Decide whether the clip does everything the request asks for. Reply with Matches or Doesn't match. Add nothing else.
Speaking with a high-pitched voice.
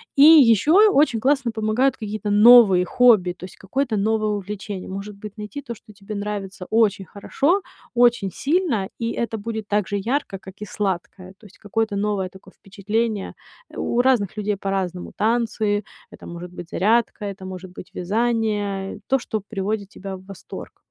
Matches